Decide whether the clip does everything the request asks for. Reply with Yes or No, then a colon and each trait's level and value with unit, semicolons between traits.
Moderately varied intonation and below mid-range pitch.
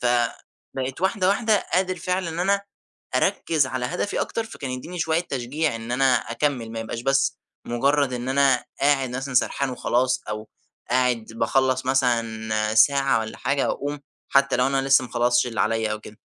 Yes: average, 3.2 semitones; low, 130 Hz